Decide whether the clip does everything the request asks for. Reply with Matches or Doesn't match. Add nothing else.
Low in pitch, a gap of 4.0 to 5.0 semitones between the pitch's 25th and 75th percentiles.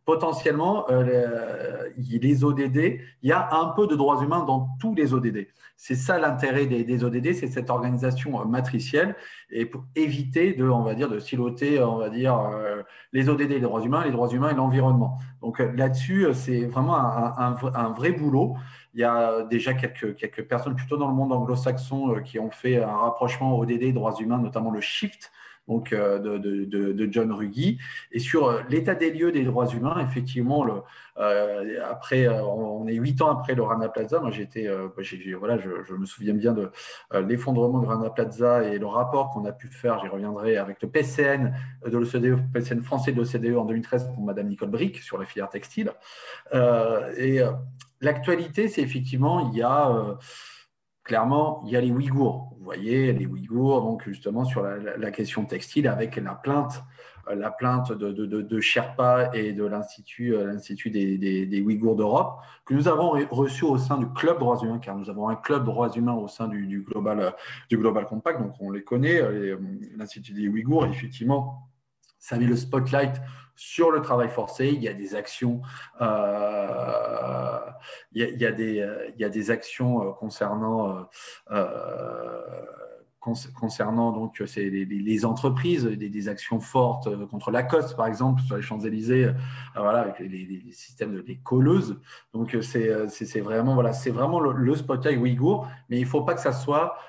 Doesn't match